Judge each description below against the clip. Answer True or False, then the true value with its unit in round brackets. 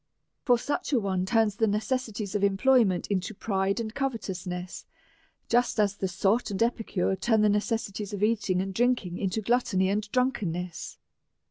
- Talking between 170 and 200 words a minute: False (160 wpm)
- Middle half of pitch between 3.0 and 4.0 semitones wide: True (3.4 semitones)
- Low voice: False (205 Hz)